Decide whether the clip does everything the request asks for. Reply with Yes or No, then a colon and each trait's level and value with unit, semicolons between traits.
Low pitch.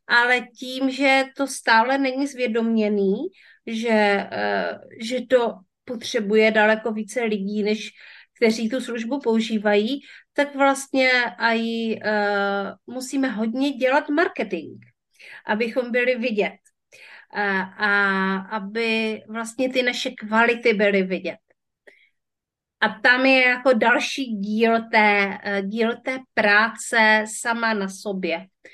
No: high, 230 Hz